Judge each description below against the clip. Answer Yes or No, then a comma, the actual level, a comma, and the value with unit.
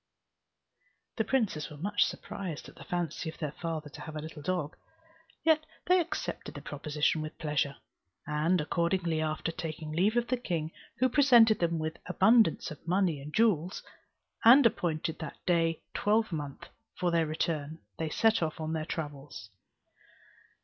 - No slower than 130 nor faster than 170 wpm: Yes, average, 155 wpm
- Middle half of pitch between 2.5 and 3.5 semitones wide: No, average, 4.9 semitones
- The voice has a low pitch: No, medium, 165 Hz